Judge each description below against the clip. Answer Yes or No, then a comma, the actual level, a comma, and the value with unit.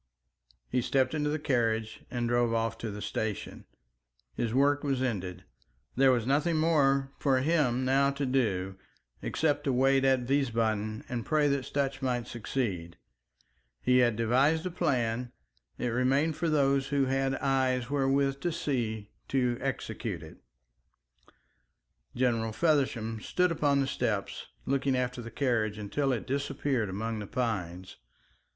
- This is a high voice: No, low, 130 Hz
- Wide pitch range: No, average, 3.3 semitones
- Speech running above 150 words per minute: No, average, 145 wpm